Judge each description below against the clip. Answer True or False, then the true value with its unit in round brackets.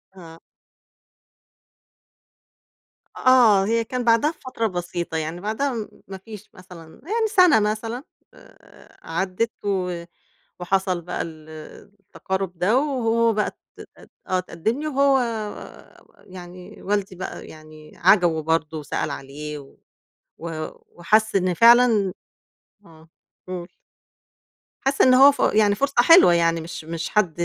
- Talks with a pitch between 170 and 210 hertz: True (190 Hz)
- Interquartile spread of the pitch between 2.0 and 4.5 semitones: False (5.4 semitones)